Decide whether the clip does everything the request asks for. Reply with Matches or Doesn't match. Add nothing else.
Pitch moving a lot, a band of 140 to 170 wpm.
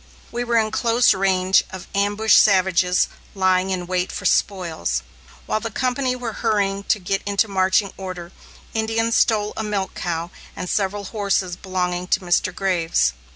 Doesn't match